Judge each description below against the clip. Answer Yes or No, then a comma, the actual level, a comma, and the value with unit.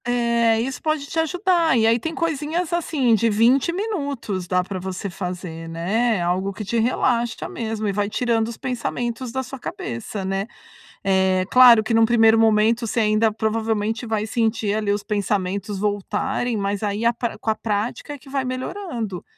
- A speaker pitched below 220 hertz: No, high, 225 Hz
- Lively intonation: No, average, 3.4 semitones